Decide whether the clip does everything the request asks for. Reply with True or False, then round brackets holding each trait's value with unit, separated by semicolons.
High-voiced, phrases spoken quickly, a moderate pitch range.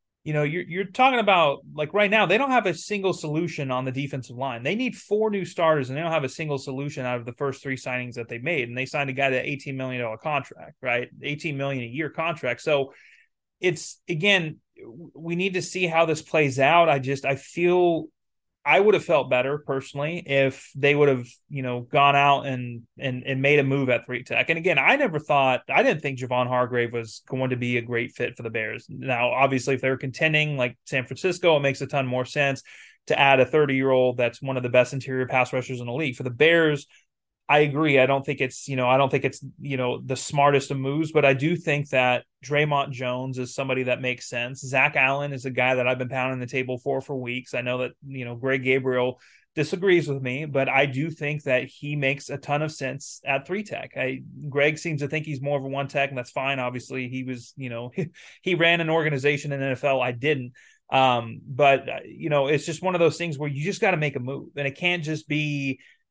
False (140 Hz; 240 wpm; 3.0 semitones)